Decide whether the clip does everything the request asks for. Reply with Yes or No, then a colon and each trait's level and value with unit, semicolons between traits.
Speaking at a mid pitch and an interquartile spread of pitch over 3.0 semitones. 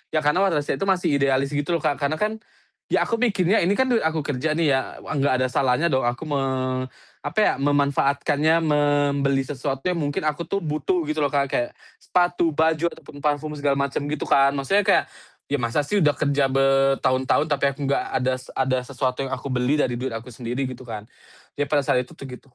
No: medium, 145 Hz; average, 2.7 semitones